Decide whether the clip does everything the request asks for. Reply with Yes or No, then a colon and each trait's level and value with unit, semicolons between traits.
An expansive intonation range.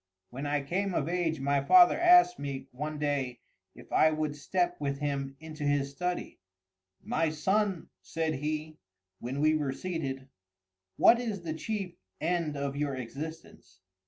No: average, 3.8 semitones